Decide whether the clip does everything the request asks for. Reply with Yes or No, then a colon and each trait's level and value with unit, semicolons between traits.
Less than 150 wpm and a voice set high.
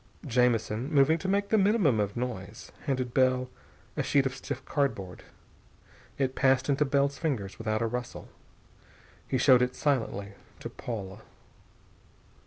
No: average, 140 wpm; low, 130 Hz